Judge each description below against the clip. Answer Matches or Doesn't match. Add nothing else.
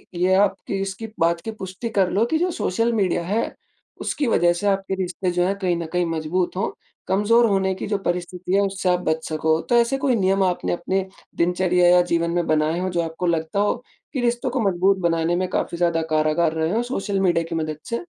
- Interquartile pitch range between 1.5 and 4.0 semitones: Matches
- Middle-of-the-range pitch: Matches